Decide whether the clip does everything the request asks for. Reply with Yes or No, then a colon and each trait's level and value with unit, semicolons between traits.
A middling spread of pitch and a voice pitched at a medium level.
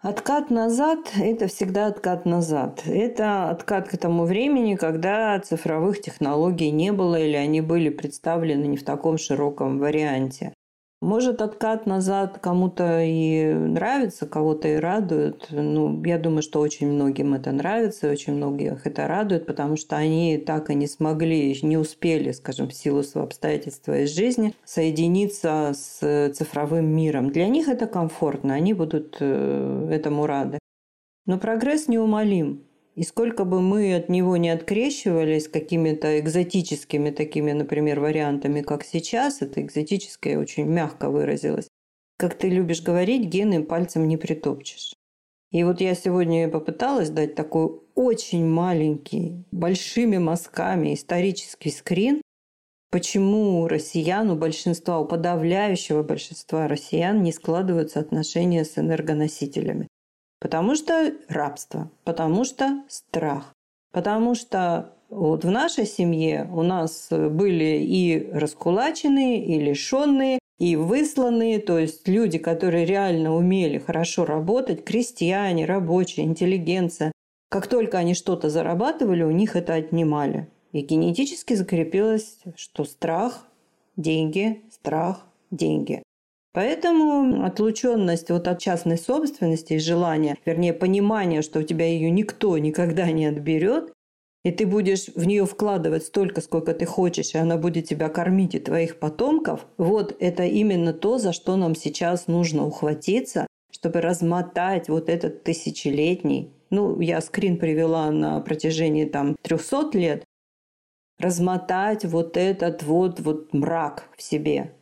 Yes: average, 4.1 semitones; medium, 170 Hz